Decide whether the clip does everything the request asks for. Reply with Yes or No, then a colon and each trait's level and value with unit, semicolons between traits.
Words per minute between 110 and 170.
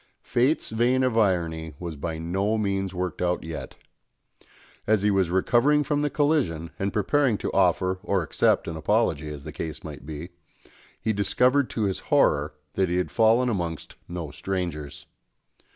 Yes: average, 165 wpm